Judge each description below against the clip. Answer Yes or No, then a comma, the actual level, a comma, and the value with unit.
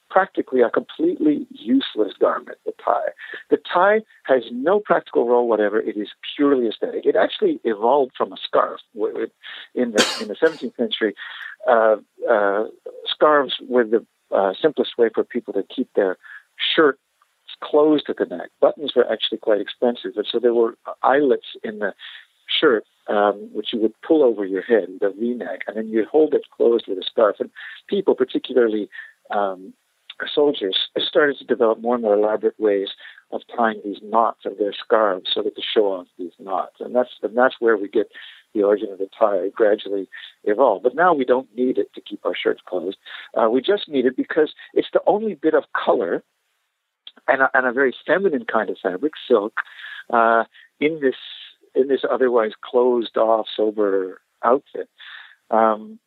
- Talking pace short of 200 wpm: Yes, average, 180 wpm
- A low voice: Yes, low, 130 Hz